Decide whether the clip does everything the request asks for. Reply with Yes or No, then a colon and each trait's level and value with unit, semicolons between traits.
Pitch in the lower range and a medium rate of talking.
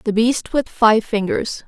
No: high, 235 Hz; average, 180 wpm